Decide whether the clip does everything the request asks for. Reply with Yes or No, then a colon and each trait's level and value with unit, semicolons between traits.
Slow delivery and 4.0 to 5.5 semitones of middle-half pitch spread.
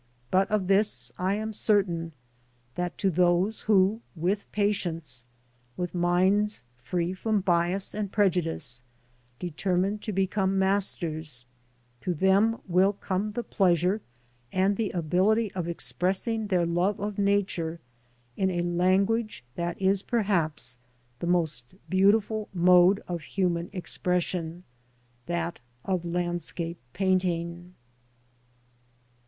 No: slow, 115 wpm; narrow, 2.6 semitones